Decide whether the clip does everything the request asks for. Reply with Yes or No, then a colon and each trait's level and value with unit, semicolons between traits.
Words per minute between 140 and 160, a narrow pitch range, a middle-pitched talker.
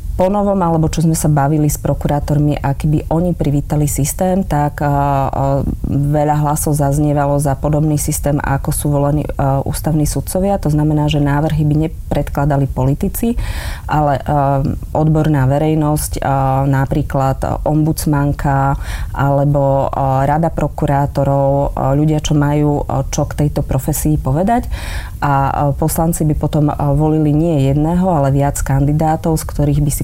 No: average, 125 wpm; narrow, 1.8 semitones; medium, 145 Hz